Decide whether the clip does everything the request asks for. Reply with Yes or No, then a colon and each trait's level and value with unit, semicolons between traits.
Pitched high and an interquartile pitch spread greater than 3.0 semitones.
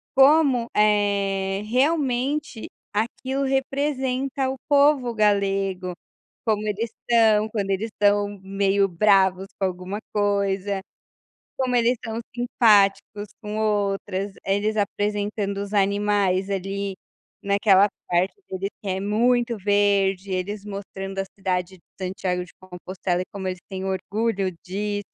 No: high, 205 Hz; narrow, 2.6 semitones